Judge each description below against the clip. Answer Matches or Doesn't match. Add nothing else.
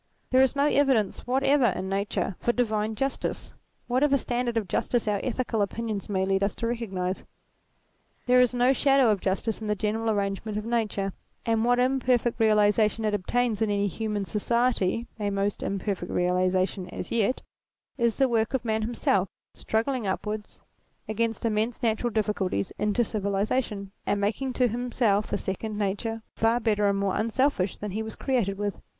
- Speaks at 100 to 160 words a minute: Doesn't match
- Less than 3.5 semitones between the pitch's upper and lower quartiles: Matches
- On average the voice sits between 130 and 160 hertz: Doesn't match